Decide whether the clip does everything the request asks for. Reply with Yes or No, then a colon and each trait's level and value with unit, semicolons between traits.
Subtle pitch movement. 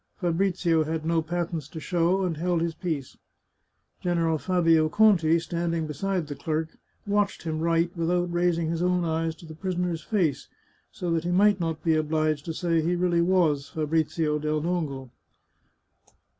Yes: narrow, 2.0 semitones